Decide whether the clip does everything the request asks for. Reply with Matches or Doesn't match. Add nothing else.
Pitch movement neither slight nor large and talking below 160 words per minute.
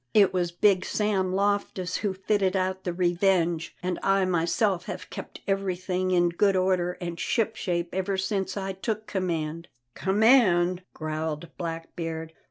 Doesn't match